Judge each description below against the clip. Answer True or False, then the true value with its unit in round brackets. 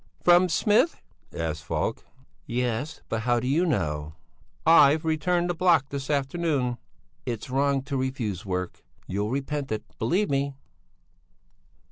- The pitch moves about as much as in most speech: False (5.9 semitones)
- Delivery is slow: True (130 wpm)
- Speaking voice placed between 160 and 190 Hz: False (135 Hz)